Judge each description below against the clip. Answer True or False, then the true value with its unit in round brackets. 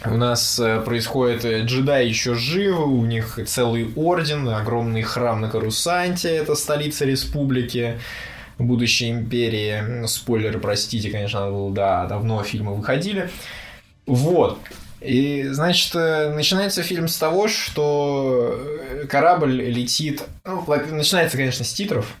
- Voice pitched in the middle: False (125 Hz)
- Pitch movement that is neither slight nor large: True (4.8 semitones)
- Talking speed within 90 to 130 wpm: True (115 wpm)